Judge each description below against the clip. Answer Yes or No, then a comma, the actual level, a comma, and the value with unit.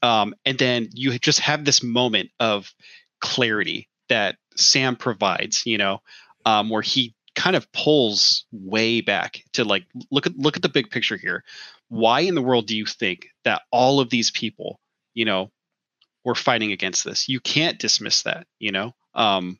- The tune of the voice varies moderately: Yes, average, 3.5 semitones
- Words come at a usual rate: Yes, average, 180 wpm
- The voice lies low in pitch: Yes, low, 120 Hz